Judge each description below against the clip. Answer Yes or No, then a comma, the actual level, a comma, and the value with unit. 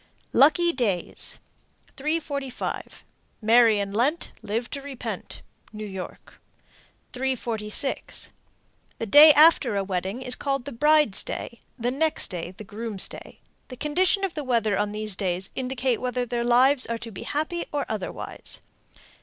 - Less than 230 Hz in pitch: No, high, 245 Hz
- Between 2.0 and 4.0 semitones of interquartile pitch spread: No, average, 5.1 semitones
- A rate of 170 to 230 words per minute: No, average, 145 wpm